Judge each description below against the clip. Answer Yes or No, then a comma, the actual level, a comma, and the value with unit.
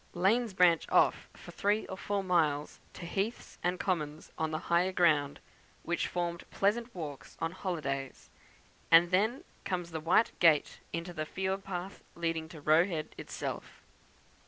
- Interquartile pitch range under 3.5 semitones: Yes, average, 3.1 semitones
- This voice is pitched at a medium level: Yes, medium, 175 Hz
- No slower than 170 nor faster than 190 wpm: No, average, 155 wpm